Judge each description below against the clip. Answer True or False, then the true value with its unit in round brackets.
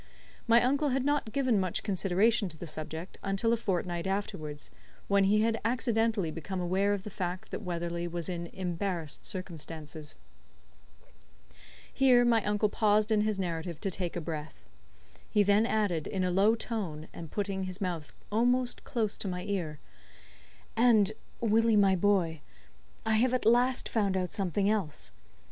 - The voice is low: False (195 Hz)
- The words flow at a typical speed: True (160 wpm)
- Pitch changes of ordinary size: True (4.2 semitones)